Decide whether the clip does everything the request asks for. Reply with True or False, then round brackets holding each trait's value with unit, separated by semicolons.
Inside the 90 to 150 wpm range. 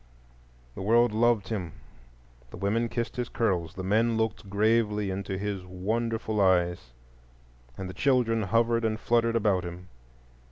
True (145 wpm)